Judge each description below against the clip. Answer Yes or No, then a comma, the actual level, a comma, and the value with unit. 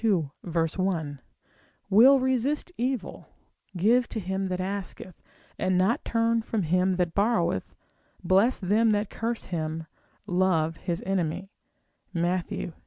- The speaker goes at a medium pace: No, slow, 115 wpm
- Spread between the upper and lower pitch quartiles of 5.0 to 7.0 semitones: No, average, 4.5 semitones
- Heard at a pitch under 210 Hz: Yes, high, 190 Hz